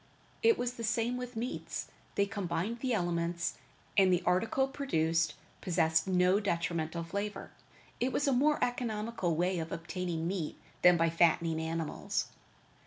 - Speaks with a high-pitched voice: No, medium, 180 Hz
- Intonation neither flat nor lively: No, wide, 5.7 semitones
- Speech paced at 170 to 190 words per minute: No, average, 145 wpm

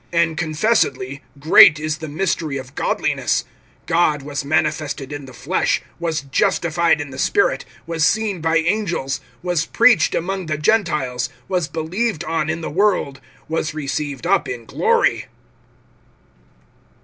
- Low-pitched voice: No, medium, 160 Hz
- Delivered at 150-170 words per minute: No, slow, 135 wpm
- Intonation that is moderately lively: Yes, average, 3.4 semitones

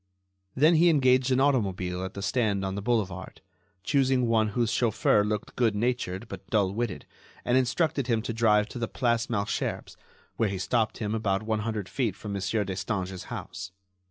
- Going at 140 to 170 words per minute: No, average, 180 wpm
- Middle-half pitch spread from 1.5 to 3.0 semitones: No, average, 3.7 semitones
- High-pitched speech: No, low, 110 Hz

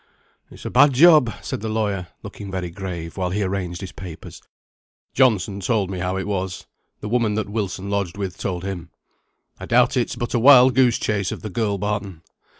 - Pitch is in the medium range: No, low, 100 Hz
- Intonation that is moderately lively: Yes, average, 3.0 semitones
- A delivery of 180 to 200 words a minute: Yes, average, 195 wpm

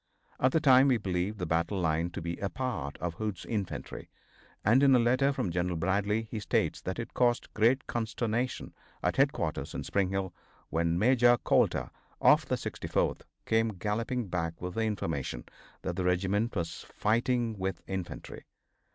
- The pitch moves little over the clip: No, average, 5.0 semitones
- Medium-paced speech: Yes, average, 170 wpm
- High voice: No, low, 105 Hz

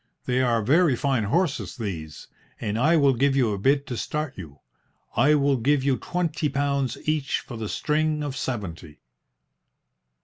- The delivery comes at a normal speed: Yes, average, 165 wpm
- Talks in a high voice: No, low, 135 Hz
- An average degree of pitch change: Yes, average, 4.7 semitones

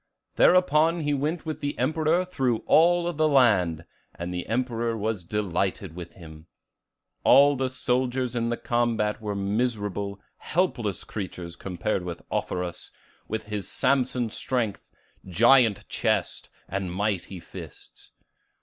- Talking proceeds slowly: Yes, slow, 125 wpm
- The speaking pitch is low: Yes, low, 115 Hz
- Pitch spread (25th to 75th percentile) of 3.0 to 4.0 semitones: No, wide, 5.6 semitones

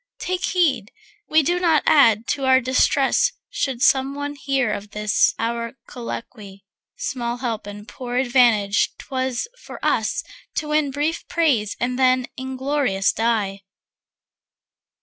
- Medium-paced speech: No, slow, 130 wpm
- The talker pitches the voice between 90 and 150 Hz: No, very high, 255 Hz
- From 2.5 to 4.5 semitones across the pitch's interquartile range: Yes, average, 3.9 semitones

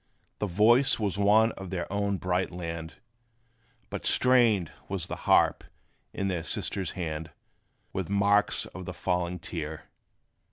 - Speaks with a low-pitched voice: Yes, very low, 95 Hz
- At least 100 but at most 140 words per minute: Yes, slow, 135 wpm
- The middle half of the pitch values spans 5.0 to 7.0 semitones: No, average, 2.9 semitones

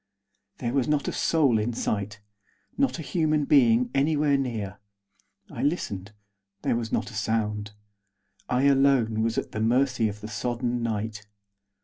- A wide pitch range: No, average, 4.3 semitones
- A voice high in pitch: No, low, 120 Hz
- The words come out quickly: No, average, 150 wpm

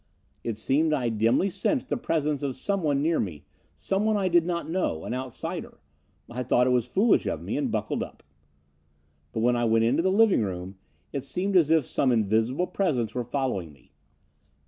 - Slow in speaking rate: No, average, 190 wpm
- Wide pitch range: Yes, wide, 7.2 semitones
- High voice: No, low, 135 Hz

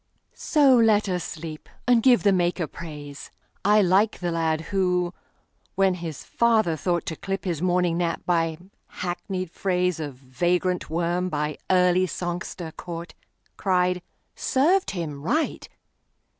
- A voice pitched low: No, medium, 180 Hz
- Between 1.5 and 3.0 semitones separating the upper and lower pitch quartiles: Yes, narrow, 2.6 semitones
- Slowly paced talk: Yes, slow, 120 wpm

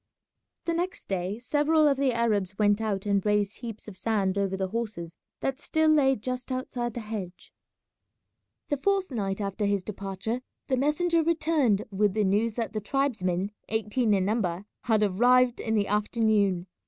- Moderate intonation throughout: Yes, average, 4.3 semitones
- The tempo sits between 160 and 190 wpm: Yes, average, 165 wpm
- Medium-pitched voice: No, high, 220 Hz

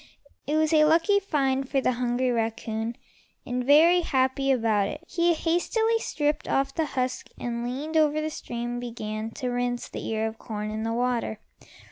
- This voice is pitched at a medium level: No, very high, 255 Hz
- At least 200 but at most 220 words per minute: No, average, 175 wpm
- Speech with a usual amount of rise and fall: Yes, average, 4.6 semitones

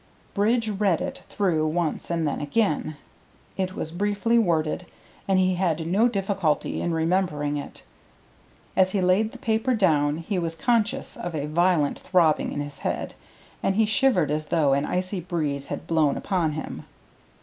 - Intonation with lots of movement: No, average, 4.5 semitones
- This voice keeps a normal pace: Yes, average, 165 wpm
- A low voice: No, medium, 175 Hz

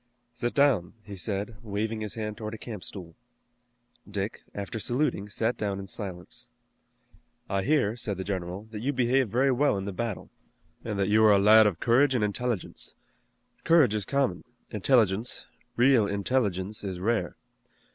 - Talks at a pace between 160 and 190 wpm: Yes, average, 165 wpm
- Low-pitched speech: Yes, low, 105 Hz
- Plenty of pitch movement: No, average, 3.4 semitones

